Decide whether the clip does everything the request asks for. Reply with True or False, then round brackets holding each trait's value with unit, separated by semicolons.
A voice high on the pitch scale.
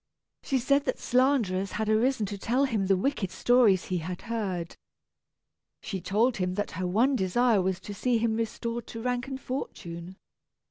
True (220 Hz)